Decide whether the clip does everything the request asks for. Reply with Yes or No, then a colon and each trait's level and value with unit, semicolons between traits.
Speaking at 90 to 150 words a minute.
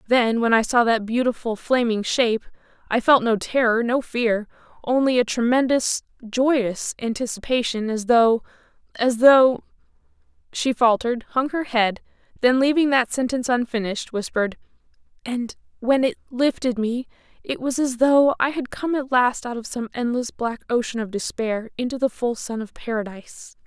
Yes: average, 140 wpm